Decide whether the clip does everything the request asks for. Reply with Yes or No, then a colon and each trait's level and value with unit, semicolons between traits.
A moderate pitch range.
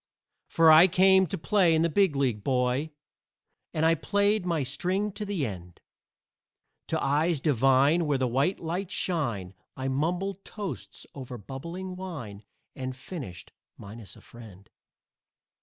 No: wide, 6.0 semitones